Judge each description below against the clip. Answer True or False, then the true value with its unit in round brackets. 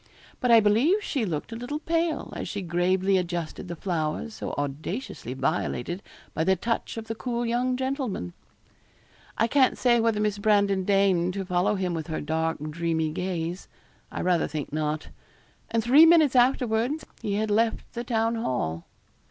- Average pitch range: False (5.8 semitones)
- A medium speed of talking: True (170 wpm)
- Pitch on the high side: True (200 Hz)